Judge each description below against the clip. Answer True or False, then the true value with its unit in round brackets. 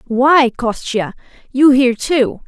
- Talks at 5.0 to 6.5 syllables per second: False (3.7 syllables/s)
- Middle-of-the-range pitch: False (255 Hz)